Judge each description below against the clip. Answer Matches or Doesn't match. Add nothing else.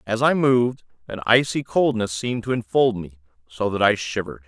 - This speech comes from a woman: Doesn't match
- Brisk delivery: Doesn't match